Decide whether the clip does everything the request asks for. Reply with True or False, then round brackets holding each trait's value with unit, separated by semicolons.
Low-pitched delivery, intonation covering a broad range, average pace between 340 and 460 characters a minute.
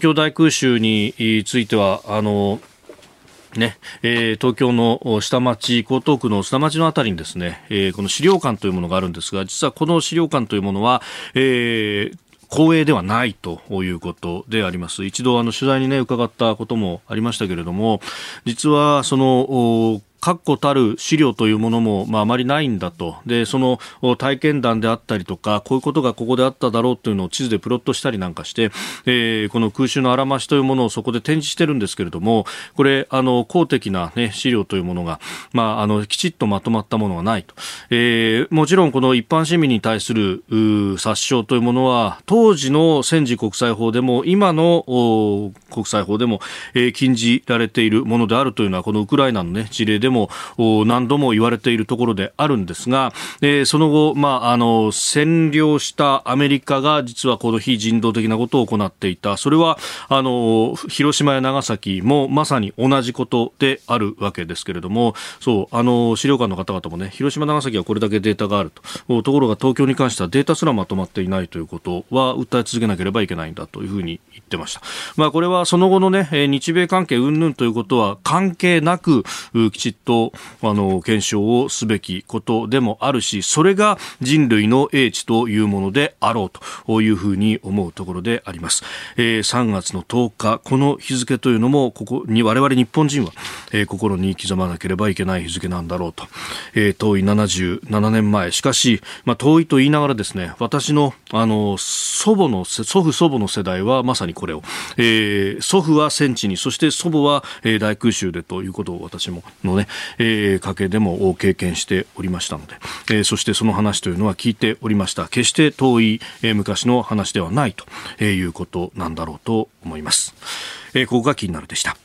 False (115 Hz; 4.6 semitones; 380 characters per minute)